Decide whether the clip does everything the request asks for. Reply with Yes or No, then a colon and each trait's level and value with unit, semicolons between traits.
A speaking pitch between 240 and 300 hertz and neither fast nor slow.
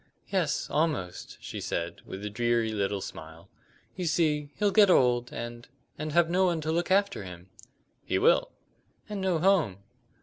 No: medium, 150 Hz; average, 165 wpm